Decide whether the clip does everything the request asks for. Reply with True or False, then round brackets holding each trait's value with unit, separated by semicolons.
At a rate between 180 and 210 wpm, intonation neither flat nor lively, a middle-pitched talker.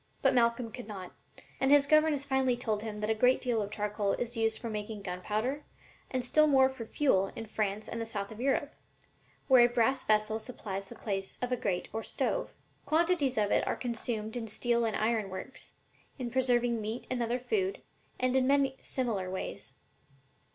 False (200 wpm; 3.5 semitones; 235 Hz)